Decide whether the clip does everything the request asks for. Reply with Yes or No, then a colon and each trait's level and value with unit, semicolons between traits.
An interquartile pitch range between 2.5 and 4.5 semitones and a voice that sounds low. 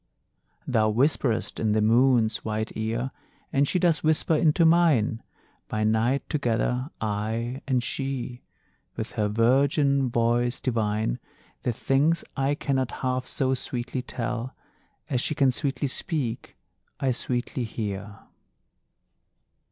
Yes: average, 3.5 semitones; low, 125 Hz